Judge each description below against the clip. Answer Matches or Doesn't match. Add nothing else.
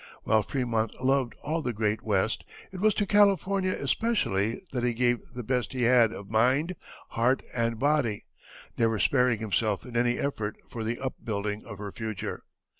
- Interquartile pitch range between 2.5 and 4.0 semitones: Matches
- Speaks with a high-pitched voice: Doesn't match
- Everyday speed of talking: Matches